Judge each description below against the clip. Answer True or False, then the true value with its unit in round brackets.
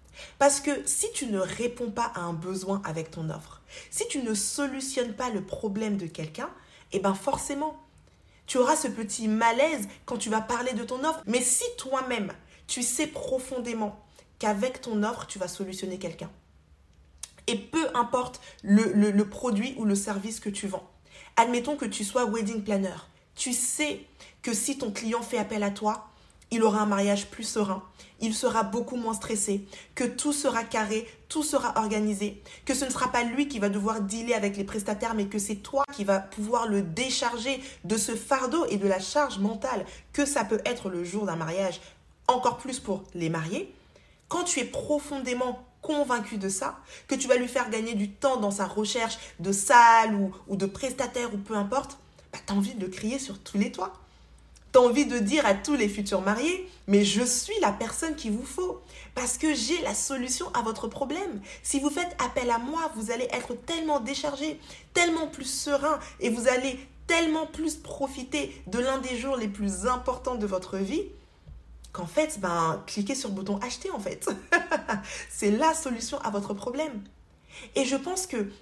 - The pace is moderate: True (190 wpm)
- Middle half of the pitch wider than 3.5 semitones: True (4.9 semitones)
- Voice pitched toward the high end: True (235 Hz)